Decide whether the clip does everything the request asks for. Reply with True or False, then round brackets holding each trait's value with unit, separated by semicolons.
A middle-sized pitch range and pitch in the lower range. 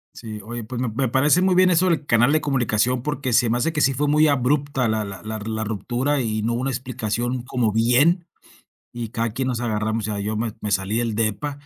True (4.0 semitones; 120 Hz)